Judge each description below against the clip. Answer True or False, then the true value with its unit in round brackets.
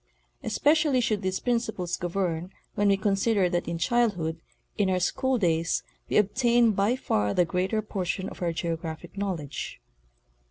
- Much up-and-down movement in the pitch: False (4.5 semitones)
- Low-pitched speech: False (195 Hz)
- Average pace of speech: True (150 wpm)